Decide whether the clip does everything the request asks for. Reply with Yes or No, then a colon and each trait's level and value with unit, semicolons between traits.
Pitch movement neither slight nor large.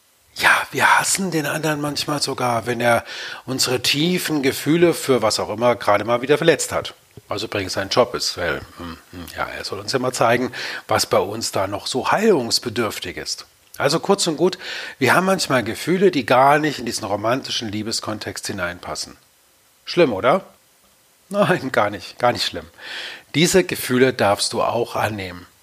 No: wide, 6.5 semitones